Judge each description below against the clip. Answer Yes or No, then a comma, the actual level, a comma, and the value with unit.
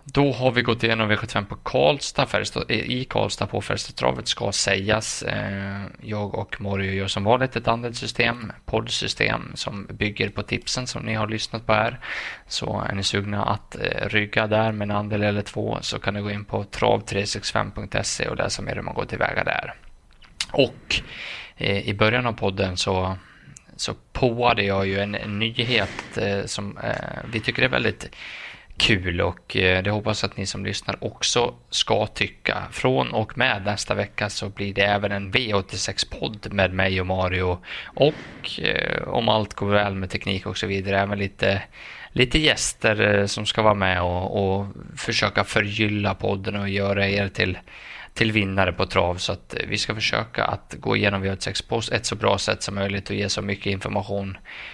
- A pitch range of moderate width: No, narrow, 2.1 semitones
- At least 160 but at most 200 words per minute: Yes, average, 175 wpm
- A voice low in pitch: Yes, low, 105 Hz